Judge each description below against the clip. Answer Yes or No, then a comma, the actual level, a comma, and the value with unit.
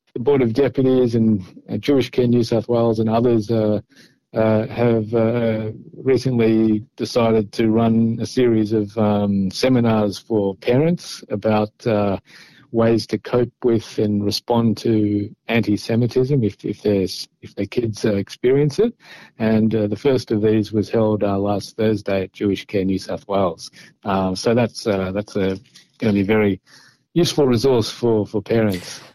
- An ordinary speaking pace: No, fast, 160 wpm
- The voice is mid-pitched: No, low, 110 Hz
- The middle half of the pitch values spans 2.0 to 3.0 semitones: Yes, narrow, 2.6 semitones